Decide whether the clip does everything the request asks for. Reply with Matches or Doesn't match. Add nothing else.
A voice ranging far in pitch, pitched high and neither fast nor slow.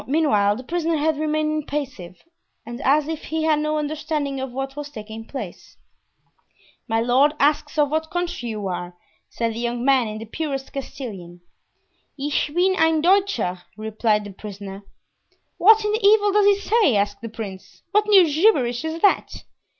Matches